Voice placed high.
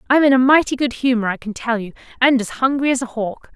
Yes: very high, 250 Hz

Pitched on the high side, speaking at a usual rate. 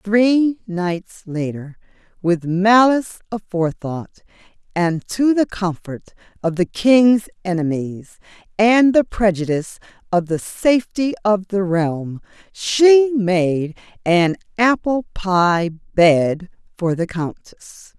No: high, 195 Hz; slow, 105 wpm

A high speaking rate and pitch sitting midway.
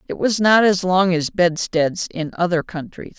No: average, 190 wpm; medium, 180 Hz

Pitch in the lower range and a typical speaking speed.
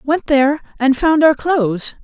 No: very high, 285 Hz; average, 175 wpm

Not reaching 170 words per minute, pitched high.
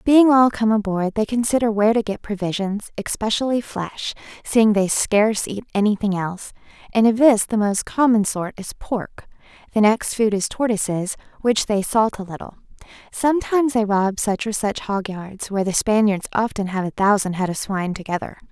No: average, 180 wpm; high, 210 Hz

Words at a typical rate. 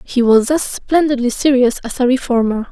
Yes: average, 175 wpm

